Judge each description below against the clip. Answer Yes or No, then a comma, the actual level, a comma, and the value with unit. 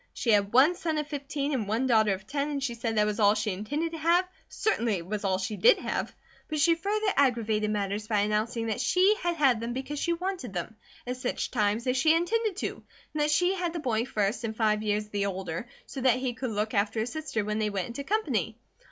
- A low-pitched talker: No, high, 240 Hz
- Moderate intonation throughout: No, wide, 6.3 semitones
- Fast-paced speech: Yes, fast, 240 wpm